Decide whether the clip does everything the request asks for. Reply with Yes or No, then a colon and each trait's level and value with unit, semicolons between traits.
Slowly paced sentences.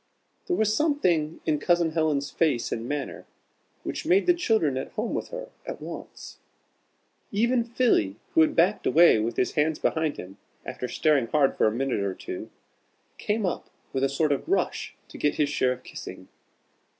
No: average, 180 wpm